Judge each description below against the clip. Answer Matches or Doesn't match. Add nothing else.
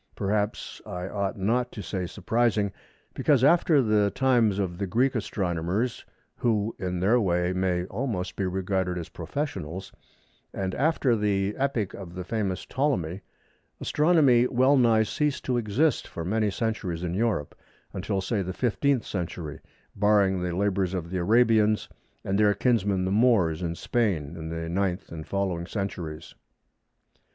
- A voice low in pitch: Matches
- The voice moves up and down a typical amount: Matches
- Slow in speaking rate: Doesn't match